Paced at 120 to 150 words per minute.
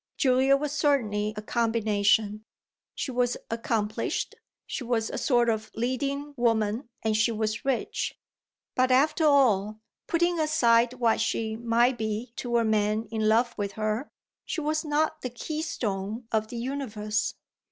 Yes: average, 145 wpm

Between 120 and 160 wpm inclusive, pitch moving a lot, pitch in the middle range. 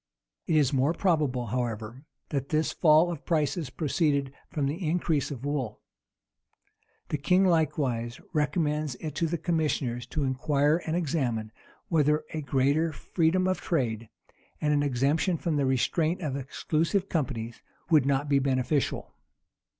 No: average, 140 wpm; average, 3.4 semitones; medium, 150 Hz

